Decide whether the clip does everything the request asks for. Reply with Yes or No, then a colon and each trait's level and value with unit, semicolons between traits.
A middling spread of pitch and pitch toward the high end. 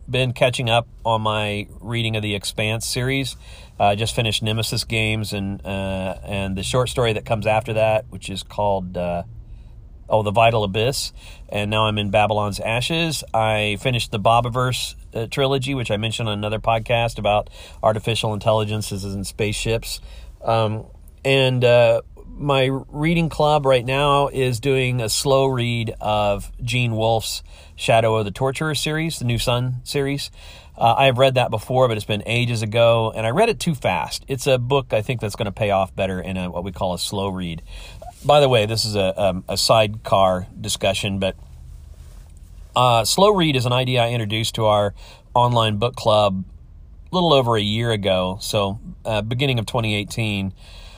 No: average, 3.8 semitones; low, 110 Hz